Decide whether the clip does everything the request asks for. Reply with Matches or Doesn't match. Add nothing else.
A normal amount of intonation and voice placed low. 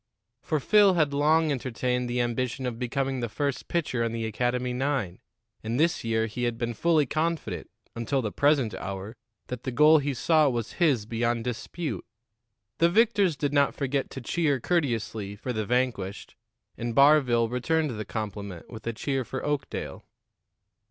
Matches